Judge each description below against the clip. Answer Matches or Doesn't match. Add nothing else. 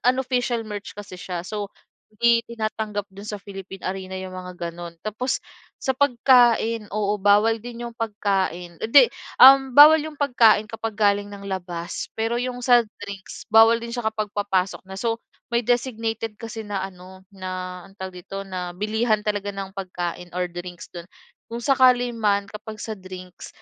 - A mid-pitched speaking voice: Doesn't match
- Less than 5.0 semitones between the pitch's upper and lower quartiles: Matches